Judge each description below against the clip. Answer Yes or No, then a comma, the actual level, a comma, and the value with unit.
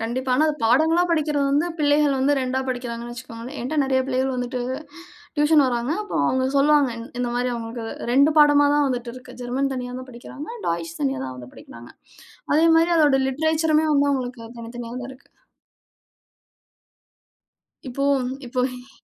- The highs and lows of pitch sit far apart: No, average, 3.2 semitones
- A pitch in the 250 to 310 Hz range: Yes, very high, 260 Hz